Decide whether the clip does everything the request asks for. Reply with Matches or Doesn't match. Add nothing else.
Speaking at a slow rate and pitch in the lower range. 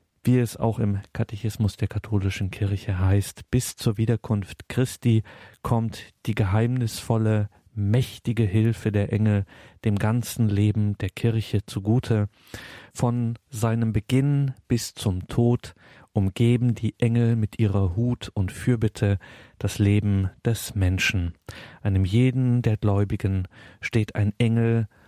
Matches